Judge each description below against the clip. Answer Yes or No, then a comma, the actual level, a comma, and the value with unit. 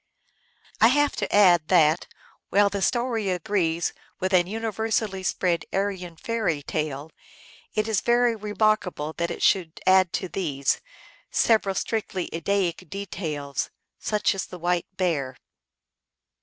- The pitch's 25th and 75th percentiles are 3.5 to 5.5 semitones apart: Yes, average, 3.9 semitones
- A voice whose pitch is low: No, medium, 185 Hz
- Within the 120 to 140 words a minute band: Yes, slow, 135 wpm